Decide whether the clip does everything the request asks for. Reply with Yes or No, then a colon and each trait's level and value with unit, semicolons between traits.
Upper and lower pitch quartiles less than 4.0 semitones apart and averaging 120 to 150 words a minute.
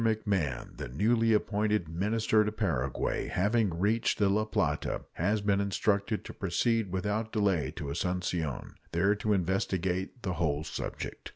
Yes: average, 3.6 semitones; average, 145 wpm